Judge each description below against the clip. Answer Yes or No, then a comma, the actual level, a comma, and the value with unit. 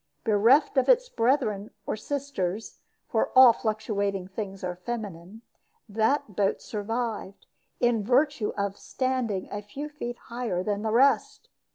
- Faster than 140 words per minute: No, slow, 135 wpm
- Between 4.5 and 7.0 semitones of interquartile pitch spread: No, average, 3.8 semitones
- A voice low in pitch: No, high, 220 Hz